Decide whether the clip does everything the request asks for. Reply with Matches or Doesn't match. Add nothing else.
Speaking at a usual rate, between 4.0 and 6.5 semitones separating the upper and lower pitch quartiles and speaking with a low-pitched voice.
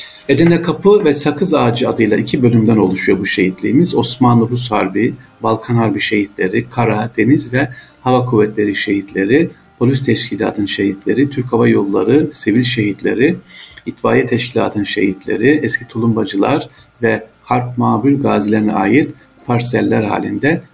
Doesn't match